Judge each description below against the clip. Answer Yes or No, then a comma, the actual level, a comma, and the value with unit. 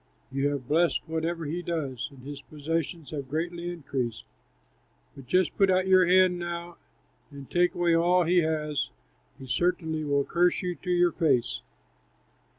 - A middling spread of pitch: Yes, average, 3.6 semitones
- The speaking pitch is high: No, medium, 165 Hz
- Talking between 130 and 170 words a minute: Yes, average, 155 wpm